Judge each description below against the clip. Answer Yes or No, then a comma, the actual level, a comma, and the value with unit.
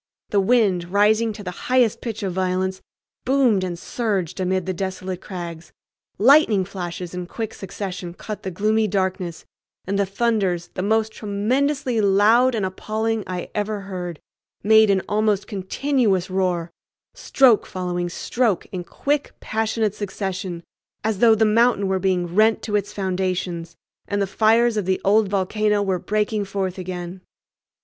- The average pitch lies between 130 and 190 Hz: No, high, 200 Hz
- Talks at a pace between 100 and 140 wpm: No, average, 150 wpm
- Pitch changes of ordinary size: Yes, average, 3.0 semitones